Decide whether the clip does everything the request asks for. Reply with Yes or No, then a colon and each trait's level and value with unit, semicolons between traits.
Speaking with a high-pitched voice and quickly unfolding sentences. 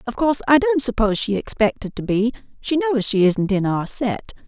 Yes: high, 235 Hz; fast, 215 wpm